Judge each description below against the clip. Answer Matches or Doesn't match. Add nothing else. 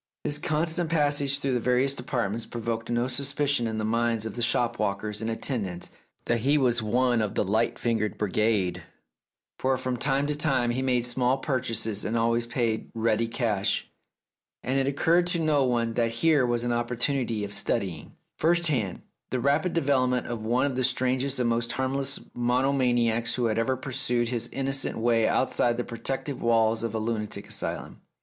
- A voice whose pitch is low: Matches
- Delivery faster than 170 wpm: Matches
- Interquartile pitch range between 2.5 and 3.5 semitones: Matches